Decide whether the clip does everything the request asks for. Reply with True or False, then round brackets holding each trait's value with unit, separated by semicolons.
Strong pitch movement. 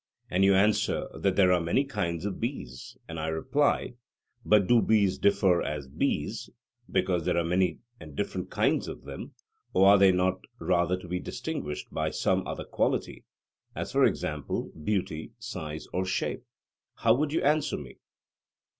False (3.6 semitones)